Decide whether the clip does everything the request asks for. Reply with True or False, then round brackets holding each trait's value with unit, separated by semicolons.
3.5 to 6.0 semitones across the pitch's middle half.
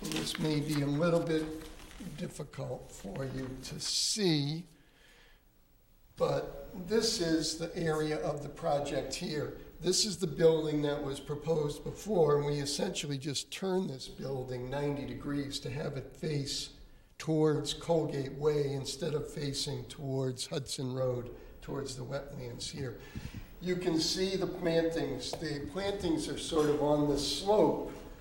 False (2.7 semitones)